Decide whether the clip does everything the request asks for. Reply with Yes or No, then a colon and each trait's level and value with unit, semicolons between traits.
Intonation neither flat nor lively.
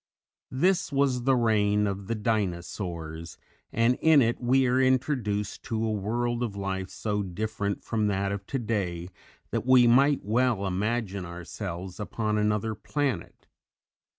Yes: average, 3.7 semitones